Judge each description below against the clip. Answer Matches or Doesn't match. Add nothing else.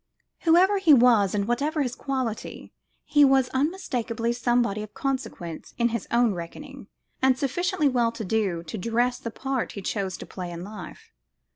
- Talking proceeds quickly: Doesn't match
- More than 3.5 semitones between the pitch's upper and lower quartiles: Matches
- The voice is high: Matches